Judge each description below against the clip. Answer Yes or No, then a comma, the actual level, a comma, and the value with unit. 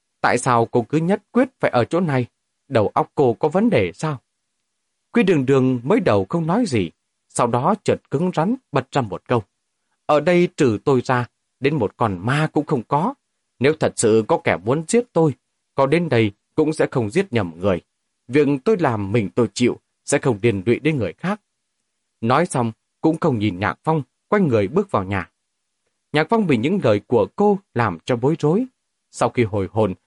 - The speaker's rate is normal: Yes, average, 205 wpm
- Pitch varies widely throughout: Yes, wide, 6.1 semitones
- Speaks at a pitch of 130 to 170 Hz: Yes, low, 135 Hz